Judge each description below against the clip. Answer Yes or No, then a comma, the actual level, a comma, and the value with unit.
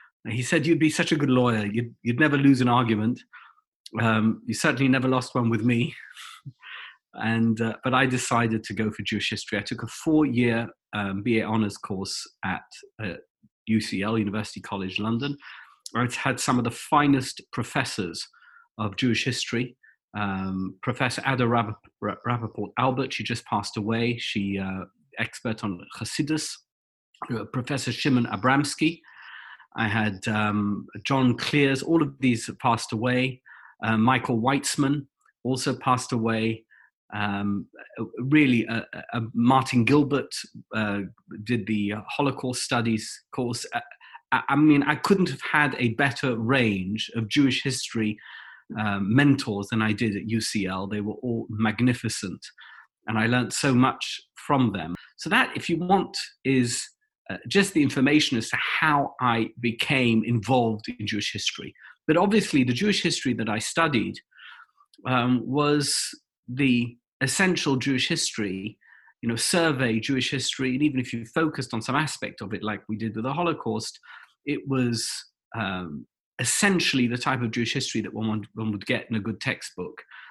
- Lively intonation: No, average, 3.9 semitones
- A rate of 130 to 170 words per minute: Yes, average, 155 wpm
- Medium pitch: No, low, 120 Hz